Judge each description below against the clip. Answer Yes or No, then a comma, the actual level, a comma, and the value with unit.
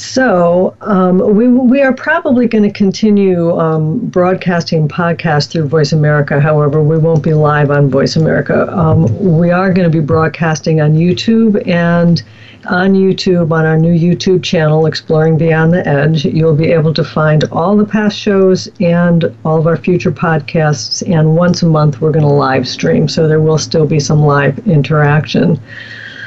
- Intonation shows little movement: No, average, 3.0 semitones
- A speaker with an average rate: Yes, average, 175 wpm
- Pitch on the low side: No, medium, 165 Hz